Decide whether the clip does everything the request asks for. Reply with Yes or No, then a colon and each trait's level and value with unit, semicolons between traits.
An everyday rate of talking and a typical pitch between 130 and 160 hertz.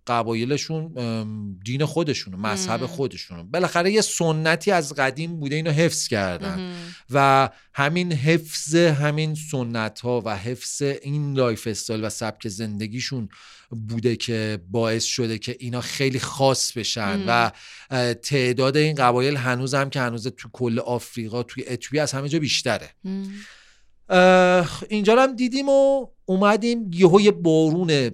Yes: average, 130 wpm; low, 135 Hz